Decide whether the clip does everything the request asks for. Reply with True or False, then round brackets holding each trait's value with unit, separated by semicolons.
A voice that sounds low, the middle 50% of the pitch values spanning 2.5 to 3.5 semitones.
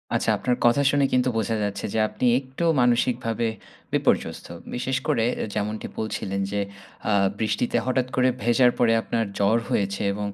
True (115 Hz; 2.9 semitones)